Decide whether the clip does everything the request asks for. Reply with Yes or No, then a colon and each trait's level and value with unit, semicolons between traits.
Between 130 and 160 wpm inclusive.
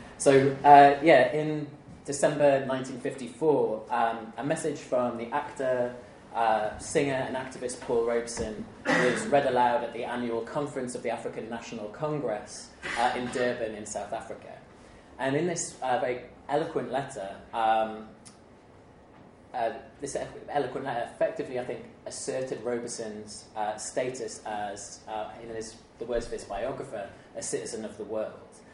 Yes: average, 145 wpm